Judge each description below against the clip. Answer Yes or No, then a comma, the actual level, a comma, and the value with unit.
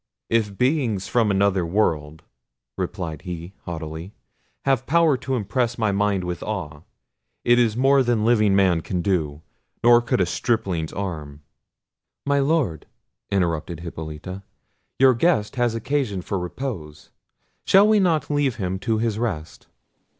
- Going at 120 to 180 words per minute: Yes, average, 140 wpm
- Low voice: Yes, low, 100 Hz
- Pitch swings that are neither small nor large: No, wide, 5.9 semitones